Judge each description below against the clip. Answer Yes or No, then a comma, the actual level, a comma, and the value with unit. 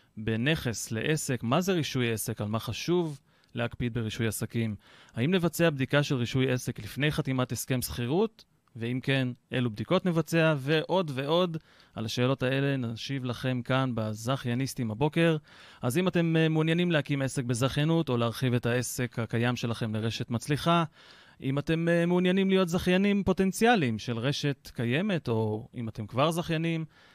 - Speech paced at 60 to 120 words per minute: No, fast, 150 wpm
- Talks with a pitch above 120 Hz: Yes, low, 135 Hz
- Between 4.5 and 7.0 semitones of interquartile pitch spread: Yes, average, 5.3 semitones